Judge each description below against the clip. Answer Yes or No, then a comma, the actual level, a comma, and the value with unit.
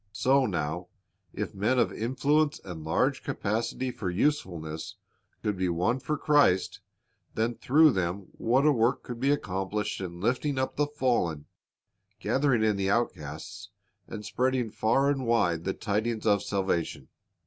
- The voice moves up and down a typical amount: No, wide, 5.8 semitones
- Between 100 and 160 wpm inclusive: Yes, average, 150 wpm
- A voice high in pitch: No, low, 110 Hz